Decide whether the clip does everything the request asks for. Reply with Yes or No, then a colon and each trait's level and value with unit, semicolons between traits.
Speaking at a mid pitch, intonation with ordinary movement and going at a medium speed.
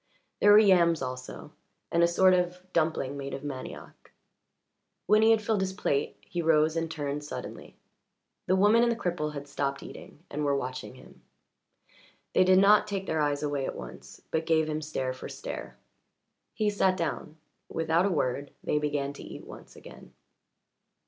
Yes: medium, 160 Hz; average, 4.6 semitones; average, 175 wpm